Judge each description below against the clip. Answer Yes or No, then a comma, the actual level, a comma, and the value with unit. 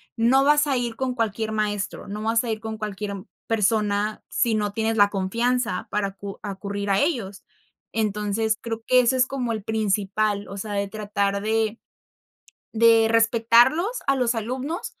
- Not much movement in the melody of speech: Yes, narrow, 2.3 semitones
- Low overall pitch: No, high, 220 Hz